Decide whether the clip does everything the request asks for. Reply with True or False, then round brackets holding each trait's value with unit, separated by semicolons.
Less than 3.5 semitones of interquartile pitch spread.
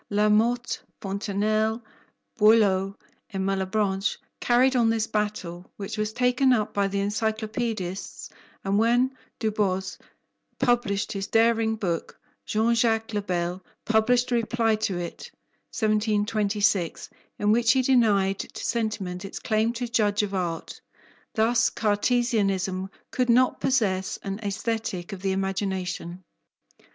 True (2.7 semitones)